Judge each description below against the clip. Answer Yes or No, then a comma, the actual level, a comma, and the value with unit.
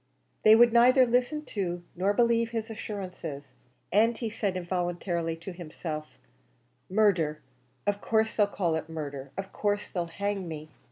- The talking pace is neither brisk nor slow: Yes, average, 150 wpm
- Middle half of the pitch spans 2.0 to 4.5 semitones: No, average, 4.9 semitones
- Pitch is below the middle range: No, high, 195 Hz